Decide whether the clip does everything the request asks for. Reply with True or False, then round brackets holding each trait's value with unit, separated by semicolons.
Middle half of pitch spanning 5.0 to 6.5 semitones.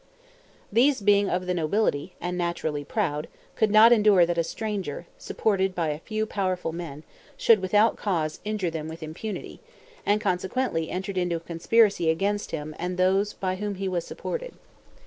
False (3.8 semitones)